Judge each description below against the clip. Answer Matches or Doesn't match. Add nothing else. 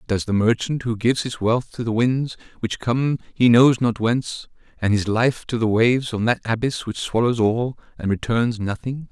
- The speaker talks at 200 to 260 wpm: Matches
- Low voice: Matches